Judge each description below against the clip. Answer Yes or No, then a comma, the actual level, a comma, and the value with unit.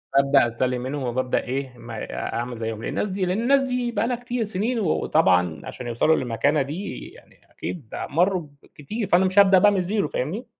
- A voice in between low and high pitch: Yes, medium, 160 Hz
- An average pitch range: No, wide, 8.5 semitones